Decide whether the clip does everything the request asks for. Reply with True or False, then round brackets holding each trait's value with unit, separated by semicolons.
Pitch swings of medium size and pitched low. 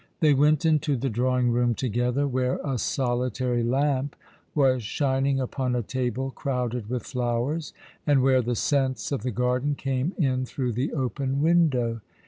False (2.2 semitones; 130 Hz)